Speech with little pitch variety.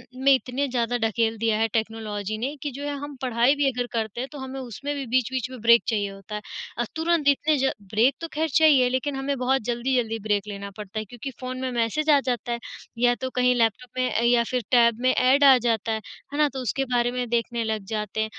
No: average, 3.1 semitones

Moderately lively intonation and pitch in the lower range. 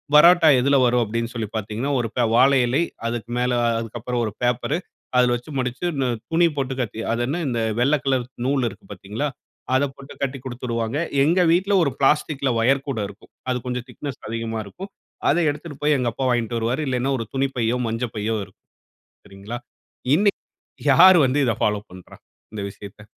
Yes: average, 3.3 semitones; low, 125 Hz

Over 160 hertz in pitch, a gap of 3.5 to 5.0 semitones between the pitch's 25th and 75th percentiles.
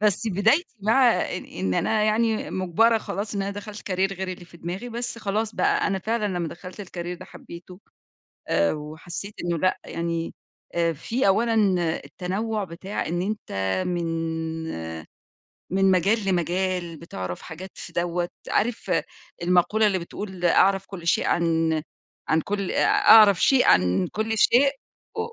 Yes: high, 190 Hz; average, 3.9 semitones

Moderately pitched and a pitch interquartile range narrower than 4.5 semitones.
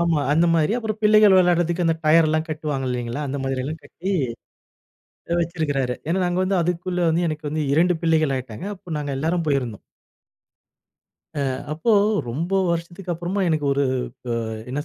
Yes: medium, 160 Hz; average, 3.4 semitones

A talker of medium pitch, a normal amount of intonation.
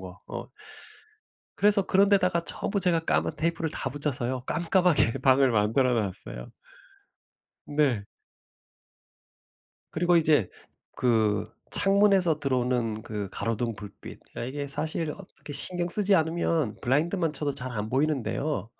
No: medium, 145 Hz; wide, 6.1 semitones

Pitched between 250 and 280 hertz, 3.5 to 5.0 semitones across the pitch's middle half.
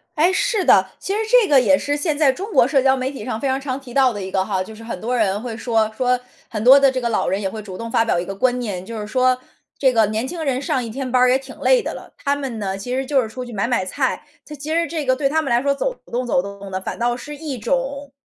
Yes: very high, 255 Hz; average, 4.1 semitones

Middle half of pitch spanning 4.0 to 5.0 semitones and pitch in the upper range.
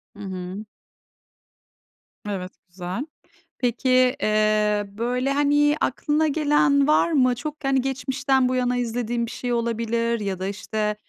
Yes: average, 4.3 semitones; high, 240 Hz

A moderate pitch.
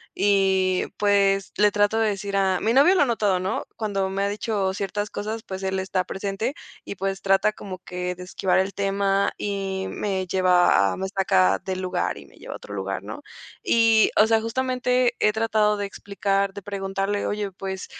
No: high, 195 Hz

